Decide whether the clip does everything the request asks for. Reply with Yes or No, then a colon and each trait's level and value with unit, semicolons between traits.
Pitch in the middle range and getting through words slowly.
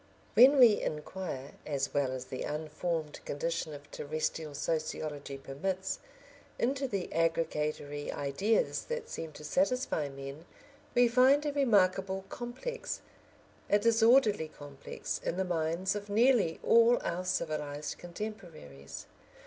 Yes: medium, 170 Hz; slow, 120 wpm